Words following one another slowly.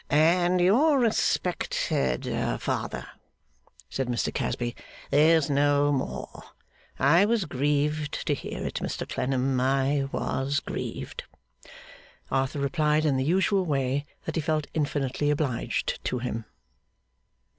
Yes: slow, 115 wpm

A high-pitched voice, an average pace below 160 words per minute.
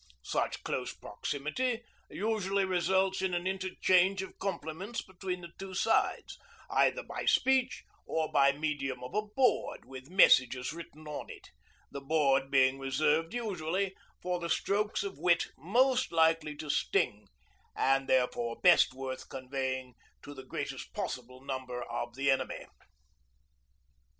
No: medium, 160 Hz; slow, 135 wpm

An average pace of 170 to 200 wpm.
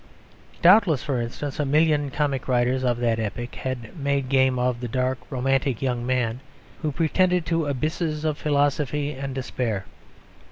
No: average, 155 wpm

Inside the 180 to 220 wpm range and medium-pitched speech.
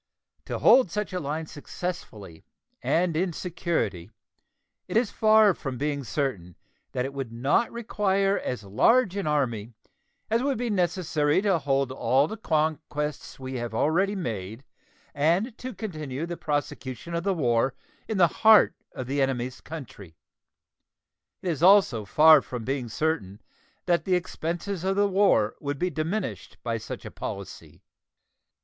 No: average, 150 wpm; medium, 155 Hz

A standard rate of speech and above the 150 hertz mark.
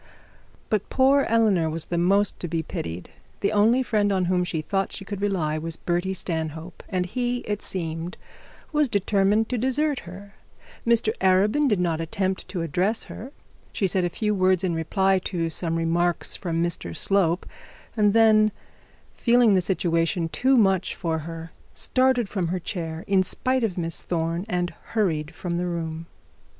Yes: average, 170 wpm; medium, 185 Hz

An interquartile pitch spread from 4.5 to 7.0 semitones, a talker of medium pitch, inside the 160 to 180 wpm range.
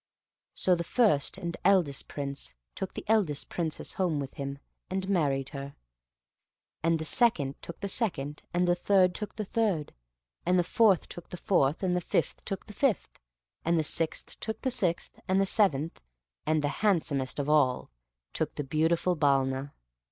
Yes: average, 5.1 semitones; medium, 170 Hz; average, 170 wpm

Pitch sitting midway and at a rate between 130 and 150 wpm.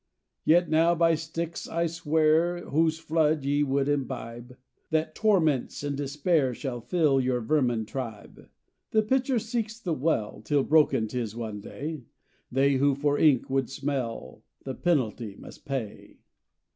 Yes: medium, 145 Hz; average, 145 wpm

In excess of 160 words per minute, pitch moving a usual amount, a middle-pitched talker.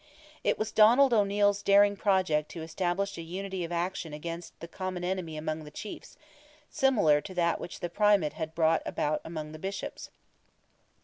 Yes: average, 170 wpm; average, 3.8 semitones; medium, 175 Hz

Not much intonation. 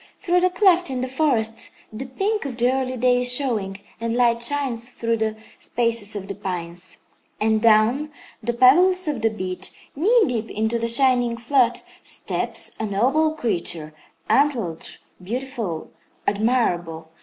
No: average, 3.8 semitones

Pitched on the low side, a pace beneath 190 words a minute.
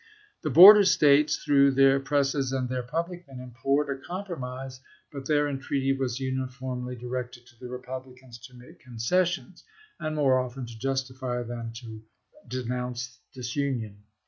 Yes: low, 130 Hz; average, 145 wpm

